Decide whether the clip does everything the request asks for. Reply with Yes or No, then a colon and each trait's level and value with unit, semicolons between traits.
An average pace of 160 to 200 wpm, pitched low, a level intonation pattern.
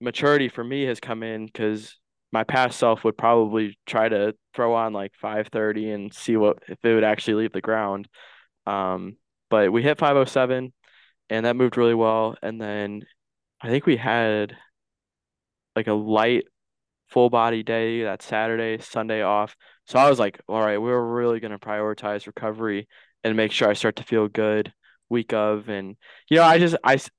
Yes: average, 185 wpm; low, 110 Hz; narrow, 1.8 semitones